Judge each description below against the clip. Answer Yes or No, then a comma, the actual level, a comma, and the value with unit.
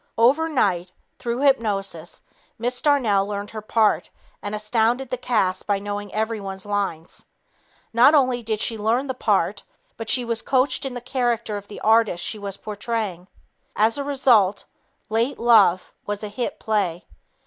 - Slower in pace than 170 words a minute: Yes, average, 155 wpm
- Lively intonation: No, average, 3.2 semitones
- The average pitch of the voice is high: Yes, high, 220 Hz